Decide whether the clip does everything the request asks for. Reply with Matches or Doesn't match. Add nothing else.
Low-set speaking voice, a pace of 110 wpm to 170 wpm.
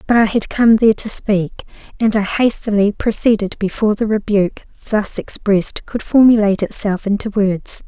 Doesn't match